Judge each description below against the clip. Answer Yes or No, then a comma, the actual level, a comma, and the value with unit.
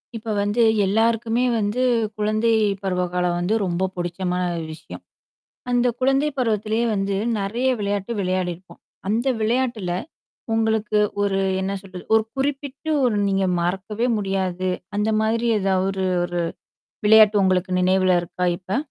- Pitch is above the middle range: Yes, high, 205 Hz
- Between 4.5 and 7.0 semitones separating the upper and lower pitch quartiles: No, average, 3.3 semitones